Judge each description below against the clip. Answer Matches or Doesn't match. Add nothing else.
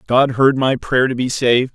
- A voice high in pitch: Doesn't match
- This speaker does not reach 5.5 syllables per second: Matches